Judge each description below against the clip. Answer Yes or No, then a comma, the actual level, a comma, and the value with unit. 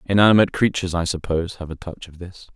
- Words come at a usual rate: No, fast, 210 wpm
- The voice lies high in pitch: No, very low, 90 Hz